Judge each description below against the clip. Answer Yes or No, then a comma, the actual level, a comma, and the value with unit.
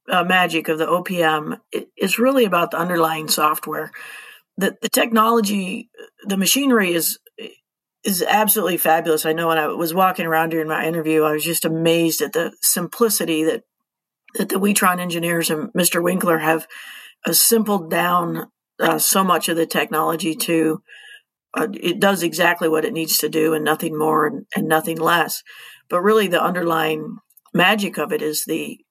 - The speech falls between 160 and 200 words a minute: Yes, average, 170 wpm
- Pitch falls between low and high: Yes, medium, 170 Hz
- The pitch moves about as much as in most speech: Yes, average, 3.6 semitones